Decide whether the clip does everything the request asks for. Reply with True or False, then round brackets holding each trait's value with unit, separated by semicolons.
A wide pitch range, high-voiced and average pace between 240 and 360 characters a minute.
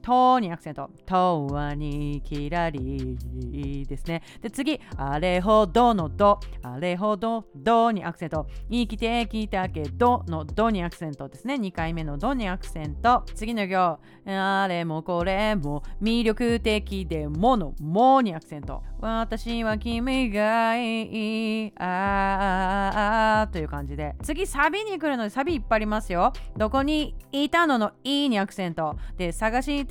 True (5.7 semitones; 210 Hz; 285 characters per minute)